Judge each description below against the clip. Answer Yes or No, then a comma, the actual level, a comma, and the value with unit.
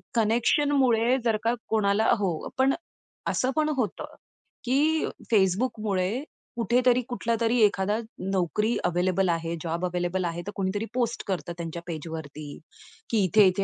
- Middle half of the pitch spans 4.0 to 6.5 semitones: Yes, average, 4.8 semitones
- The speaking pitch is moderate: No, high, 205 Hz